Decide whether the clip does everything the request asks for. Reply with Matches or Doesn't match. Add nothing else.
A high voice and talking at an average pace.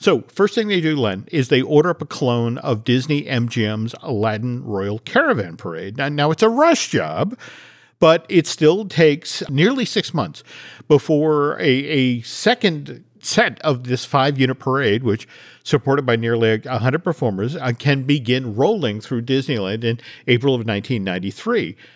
Doesn't match